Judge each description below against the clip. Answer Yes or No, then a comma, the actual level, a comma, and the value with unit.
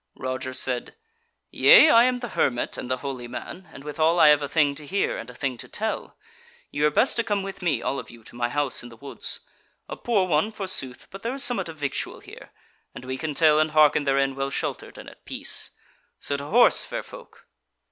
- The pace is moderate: No, fast, 230 wpm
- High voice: No, medium, 150 Hz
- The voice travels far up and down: Yes, wide, 6.4 semitones